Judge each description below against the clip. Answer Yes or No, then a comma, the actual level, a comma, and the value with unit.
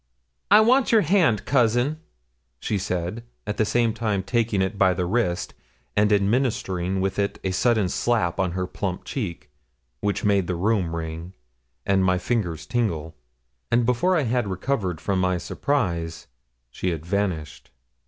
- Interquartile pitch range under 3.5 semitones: No, average, 4.7 semitones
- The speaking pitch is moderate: No, low, 100 Hz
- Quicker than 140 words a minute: Yes, average, 155 wpm